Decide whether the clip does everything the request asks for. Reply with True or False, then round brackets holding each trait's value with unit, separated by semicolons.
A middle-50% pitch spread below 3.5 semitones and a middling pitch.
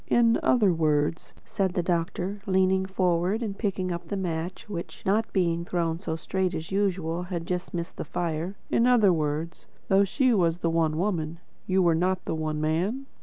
True (2.8 semitones; 180 Hz)